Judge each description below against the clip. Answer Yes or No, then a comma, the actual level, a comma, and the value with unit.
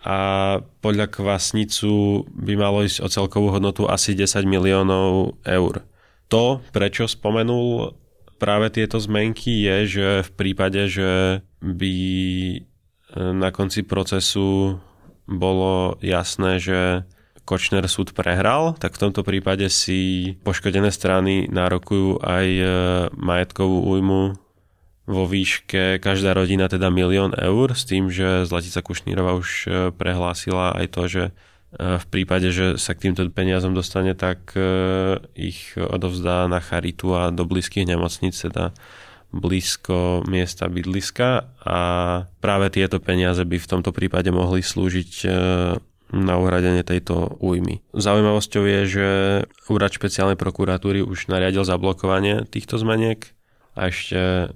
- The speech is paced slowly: No, average, 120 wpm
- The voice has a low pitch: Yes, very low, 95 Hz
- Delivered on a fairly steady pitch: Yes, narrow, 1.5 semitones